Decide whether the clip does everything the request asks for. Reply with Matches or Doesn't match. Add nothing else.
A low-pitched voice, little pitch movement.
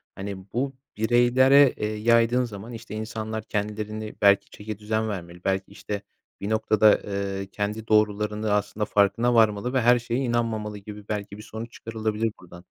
Matches